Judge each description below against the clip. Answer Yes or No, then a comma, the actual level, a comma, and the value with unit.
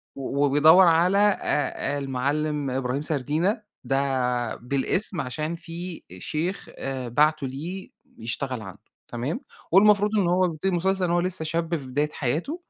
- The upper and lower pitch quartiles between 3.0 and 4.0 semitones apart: No, average, 4.8 semitones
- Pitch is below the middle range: No, medium, 155 Hz